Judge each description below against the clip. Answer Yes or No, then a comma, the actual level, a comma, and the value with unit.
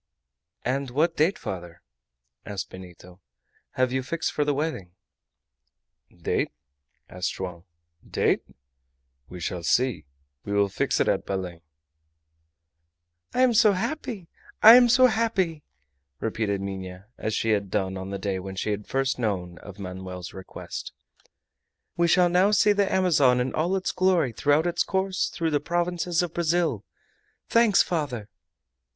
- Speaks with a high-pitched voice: No, low, 130 Hz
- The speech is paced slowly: No, average, 145 wpm